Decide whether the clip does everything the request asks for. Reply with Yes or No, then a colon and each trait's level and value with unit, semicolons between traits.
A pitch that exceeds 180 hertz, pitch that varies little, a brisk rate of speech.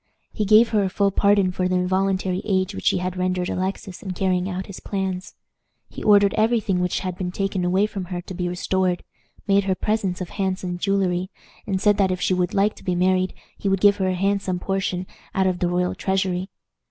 Yes: high, 190 Hz; narrow, 1.4 semitones; fast, 220 wpm